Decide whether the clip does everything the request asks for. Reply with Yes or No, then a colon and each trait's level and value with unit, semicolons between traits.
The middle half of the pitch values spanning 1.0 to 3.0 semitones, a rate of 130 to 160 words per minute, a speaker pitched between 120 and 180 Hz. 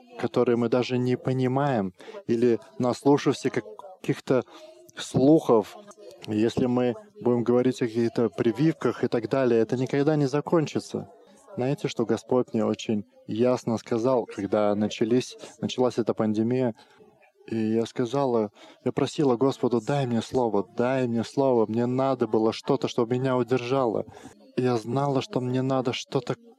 Yes: narrow, 2.6 semitones; average, 140 wpm; low, 125 Hz